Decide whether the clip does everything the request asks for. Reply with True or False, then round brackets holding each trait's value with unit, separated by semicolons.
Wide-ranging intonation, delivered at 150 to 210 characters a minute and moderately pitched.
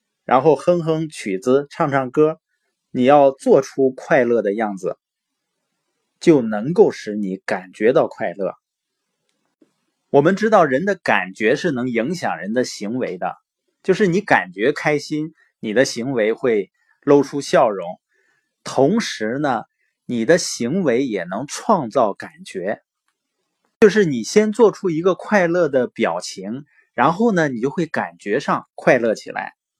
True (6.2 semitones; 200 characters per minute; 155 Hz)